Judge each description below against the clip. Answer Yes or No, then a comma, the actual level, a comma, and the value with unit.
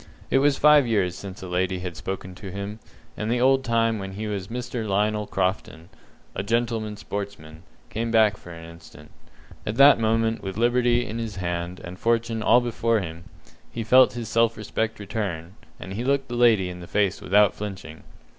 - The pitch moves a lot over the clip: No, average, 3.7 semitones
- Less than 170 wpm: No, average, 195 wpm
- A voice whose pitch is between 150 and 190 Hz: No, low, 105 Hz